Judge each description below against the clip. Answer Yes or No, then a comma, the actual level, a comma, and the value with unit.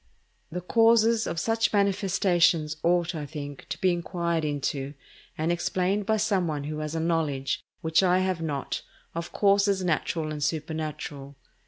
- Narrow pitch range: No, average, 3.8 semitones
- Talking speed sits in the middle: Yes, average, 155 wpm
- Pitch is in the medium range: Yes, medium, 170 Hz